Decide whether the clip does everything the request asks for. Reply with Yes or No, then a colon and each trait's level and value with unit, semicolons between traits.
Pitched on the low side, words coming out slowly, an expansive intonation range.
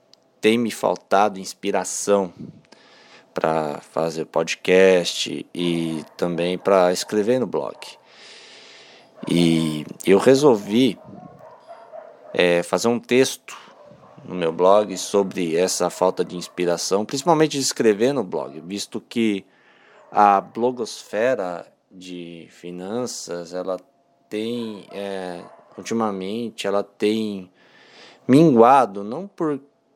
No: very low, 95 Hz; slow, 95 wpm; average, 4.3 semitones